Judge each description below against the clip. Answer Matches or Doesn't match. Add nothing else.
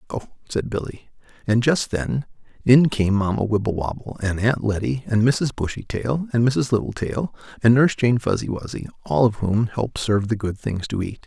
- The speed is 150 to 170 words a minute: Doesn't match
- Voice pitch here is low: Matches